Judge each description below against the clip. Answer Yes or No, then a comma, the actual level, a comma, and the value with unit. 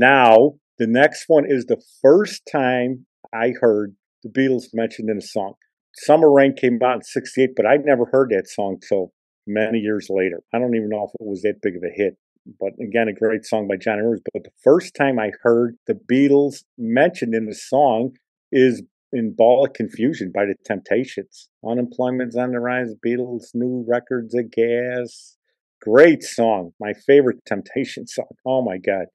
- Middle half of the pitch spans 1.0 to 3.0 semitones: Yes, narrow, 2.5 semitones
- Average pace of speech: Yes, average, 185 wpm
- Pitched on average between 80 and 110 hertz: No, low, 120 Hz